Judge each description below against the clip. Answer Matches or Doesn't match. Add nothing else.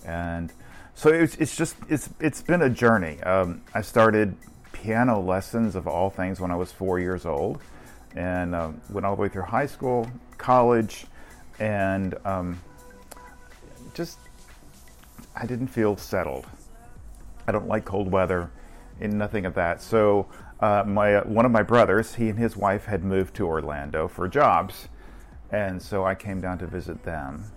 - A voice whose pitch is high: Doesn't match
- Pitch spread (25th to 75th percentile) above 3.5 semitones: Matches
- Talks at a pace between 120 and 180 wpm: Matches